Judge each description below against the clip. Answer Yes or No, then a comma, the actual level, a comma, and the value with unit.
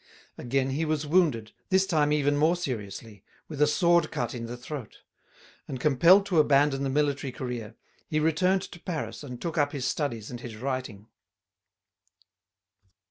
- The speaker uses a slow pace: No, average, 160 wpm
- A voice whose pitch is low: No, medium, 145 Hz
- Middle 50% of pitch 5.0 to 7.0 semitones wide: No, average, 4.2 semitones